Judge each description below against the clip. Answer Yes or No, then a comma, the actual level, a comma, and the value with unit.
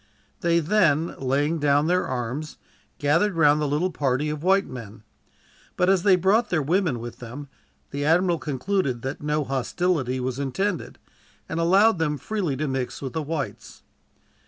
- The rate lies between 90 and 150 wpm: No, average, 160 wpm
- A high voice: No, medium, 150 Hz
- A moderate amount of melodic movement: Yes, average, 4.7 semitones